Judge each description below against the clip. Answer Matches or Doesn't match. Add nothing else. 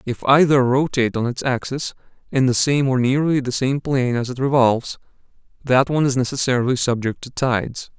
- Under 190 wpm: Matches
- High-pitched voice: Doesn't match